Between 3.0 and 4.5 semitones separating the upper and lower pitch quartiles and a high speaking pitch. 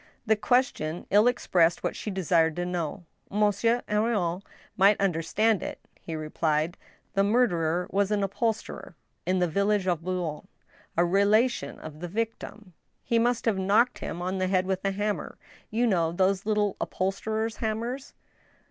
Yes: average, 3.6 semitones; high, 195 Hz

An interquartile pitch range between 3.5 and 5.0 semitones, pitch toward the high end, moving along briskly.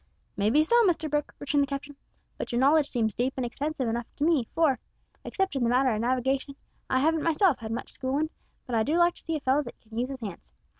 Yes: average, 4.1 semitones; very high, 270 Hz; fast, 245 wpm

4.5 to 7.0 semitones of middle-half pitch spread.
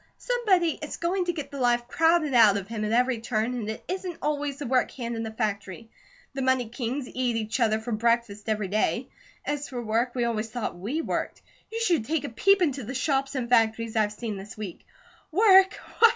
Yes: average, 4.9 semitones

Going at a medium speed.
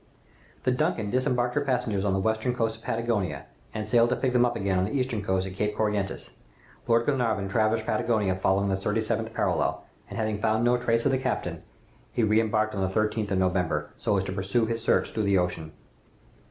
No: fast, 215 wpm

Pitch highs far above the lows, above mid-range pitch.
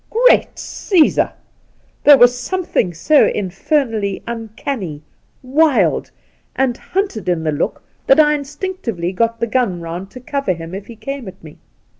Yes: wide, 7.4 semitones; high, 235 Hz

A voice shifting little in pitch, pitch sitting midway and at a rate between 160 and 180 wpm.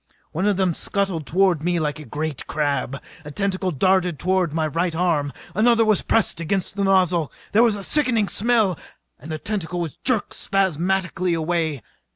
No: average, 3.7 semitones; medium, 180 Hz; average, 175 wpm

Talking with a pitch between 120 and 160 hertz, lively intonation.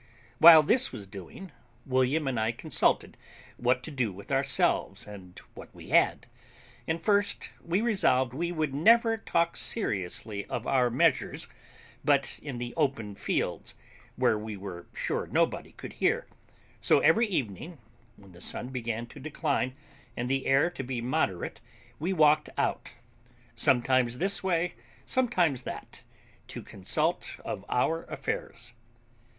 Yes: low, 135 Hz; wide, 6.1 semitones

